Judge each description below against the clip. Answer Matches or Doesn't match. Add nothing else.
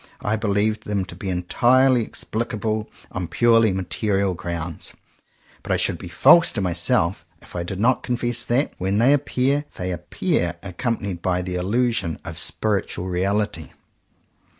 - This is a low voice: Matches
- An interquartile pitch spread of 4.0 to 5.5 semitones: Matches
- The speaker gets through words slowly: Doesn't match